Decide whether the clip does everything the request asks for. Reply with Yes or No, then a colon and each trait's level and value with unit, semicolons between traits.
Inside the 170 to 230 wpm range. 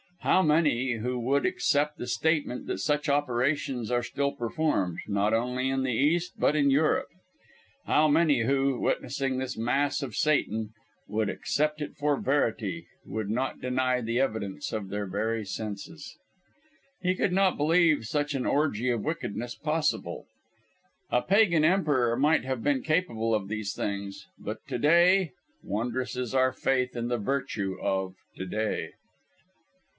No: average, 150 wpm